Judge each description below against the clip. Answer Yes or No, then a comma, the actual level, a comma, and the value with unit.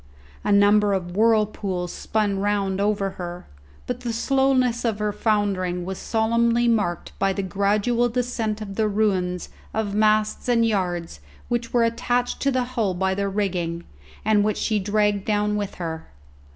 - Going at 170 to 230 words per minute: No, average, 160 wpm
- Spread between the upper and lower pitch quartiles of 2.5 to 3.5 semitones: Yes, average, 2.9 semitones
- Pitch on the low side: No, high, 210 Hz